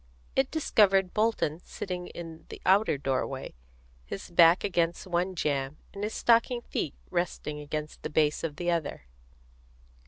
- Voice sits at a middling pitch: Yes, medium, 170 Hz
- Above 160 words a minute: No, average, 145 wpm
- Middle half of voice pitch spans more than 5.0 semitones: No, average, 4.3 semitones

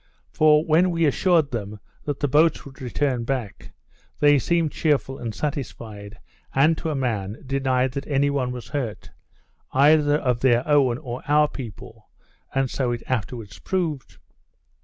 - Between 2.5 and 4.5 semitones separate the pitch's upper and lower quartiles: Yes, average, 3.7 semitones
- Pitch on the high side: No, low, 135 Hz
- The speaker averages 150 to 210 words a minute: Yes, average, 155 wpm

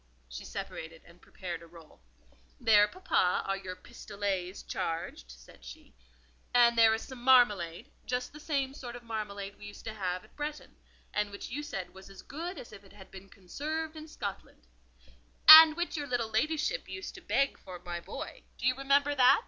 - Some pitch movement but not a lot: No, wide, 6.7 semitones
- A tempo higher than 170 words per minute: Yes, average, 185 wpm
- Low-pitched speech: No, high, 220 Hz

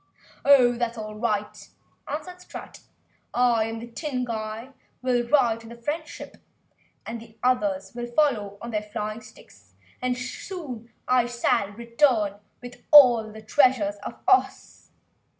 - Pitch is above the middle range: Yes, high, 235 Hz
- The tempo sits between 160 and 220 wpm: No, average, 145 wpm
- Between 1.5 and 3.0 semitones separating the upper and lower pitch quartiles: Yes, average, 2.7 semitones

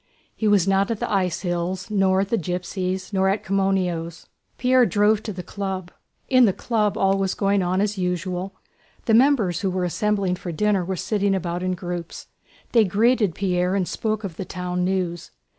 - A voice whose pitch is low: No, high, 190 Hz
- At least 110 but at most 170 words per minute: No, average, 190 wpm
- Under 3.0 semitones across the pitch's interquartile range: Yes, narrow, 2.4 semitones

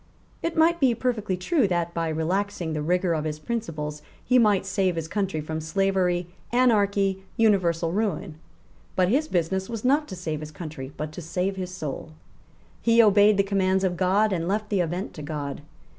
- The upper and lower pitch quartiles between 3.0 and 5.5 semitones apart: Yes, average, 4.1 semitones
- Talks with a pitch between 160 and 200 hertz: Yes, medium, 185 Hz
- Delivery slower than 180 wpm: No, average, 185 wpm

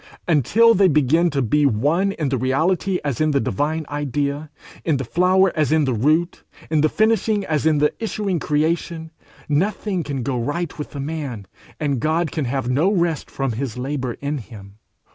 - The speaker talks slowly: No, average, 185 wpm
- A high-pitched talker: No, medium, 150 Hz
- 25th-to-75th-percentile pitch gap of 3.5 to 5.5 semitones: Yes, average, 3.9 semitones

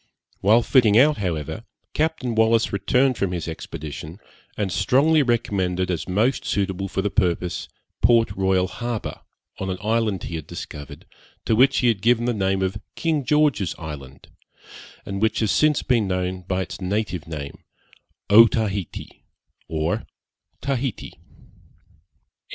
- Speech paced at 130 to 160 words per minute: Yes, average, 140 wpm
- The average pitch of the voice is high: No, low, 100 Hz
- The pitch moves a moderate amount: Yes, average, 4.5 semitones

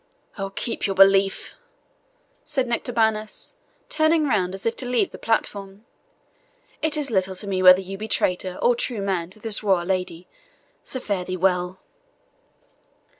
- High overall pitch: Yes, high, 195 Hz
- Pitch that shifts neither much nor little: Yes, average, 3.6 semitones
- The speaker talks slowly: No, average, 155 wpm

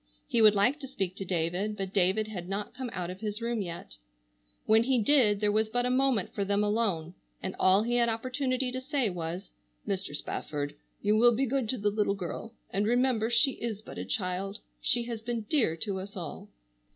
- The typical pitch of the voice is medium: No, high, 215 Hz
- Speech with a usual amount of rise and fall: Yes, average, 3.9 semitones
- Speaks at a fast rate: Yes, fast, 210 wpm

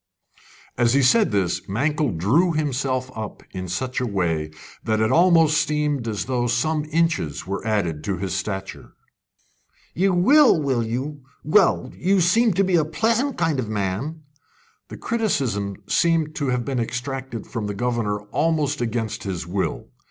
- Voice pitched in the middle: No, low, 130 Hz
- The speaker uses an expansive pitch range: Yes, wide, 7.1 semitones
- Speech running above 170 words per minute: No, average, 160 wpm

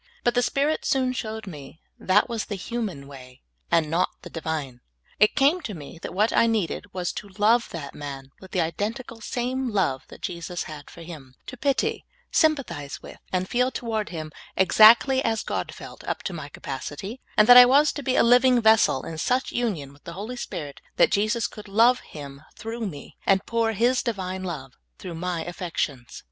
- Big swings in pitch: Yes, wide, 6.8 semitones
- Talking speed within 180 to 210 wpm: Yes, average, 190 wpm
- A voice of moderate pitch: No, high, 200 Hz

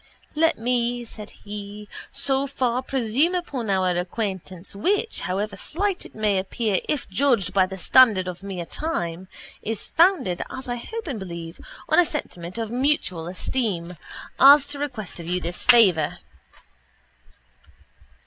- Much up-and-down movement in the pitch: Yes, wide, 6.5 semitones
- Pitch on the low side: No, high, 220 Hz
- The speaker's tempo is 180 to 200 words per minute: No, average, 145 wpm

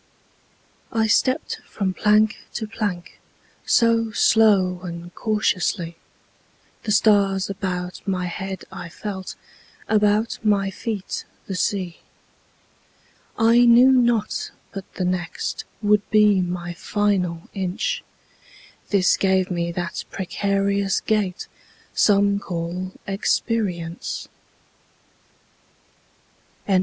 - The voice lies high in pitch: Yes, high, 195 Hz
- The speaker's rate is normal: No, slow, 95 wpm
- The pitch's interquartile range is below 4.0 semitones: Yes, average, 2.9 semitones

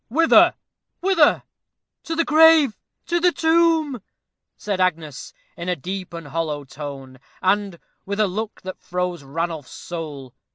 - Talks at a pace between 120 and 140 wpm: Yes, slow, 135 wpm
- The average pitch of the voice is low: No, medium, 185 Hz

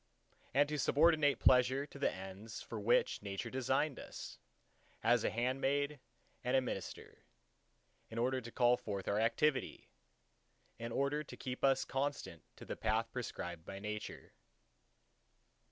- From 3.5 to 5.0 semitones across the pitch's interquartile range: Yes, average, 4.2 semitones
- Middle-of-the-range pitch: No, low, 125 Hz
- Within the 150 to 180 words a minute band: No, average, 140 wpm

